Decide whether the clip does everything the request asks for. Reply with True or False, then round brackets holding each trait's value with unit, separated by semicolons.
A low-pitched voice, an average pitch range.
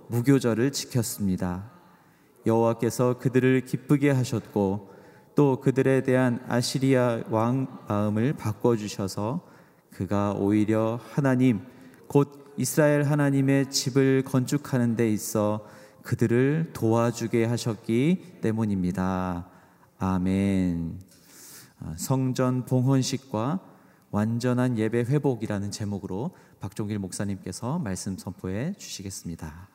True (115 Hz; 4.5 semitones)